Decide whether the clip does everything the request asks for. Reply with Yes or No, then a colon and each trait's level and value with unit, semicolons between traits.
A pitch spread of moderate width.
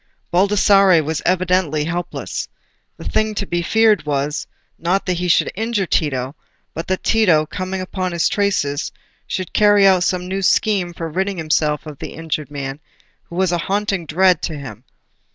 Yes: average, 4.0 semitones